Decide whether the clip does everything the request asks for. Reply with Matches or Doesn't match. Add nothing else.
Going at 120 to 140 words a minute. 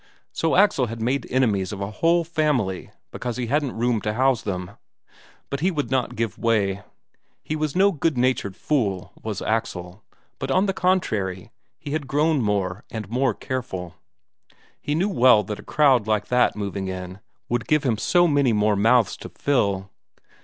Doesn't match